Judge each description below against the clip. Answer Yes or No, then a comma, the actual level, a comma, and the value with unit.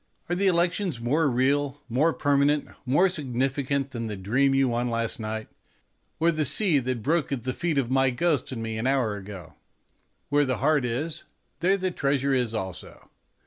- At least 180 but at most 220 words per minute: Yes, average, 185 wpm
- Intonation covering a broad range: No, average, 4.0 semitones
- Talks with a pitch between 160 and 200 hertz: No, low, 135 Hz